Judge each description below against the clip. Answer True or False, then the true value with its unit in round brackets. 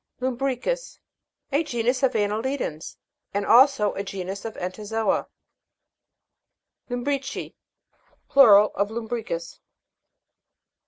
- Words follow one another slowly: True (85 wpm)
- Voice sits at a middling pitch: False (225 Hz)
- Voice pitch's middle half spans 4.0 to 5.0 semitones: True (4.5 semitones)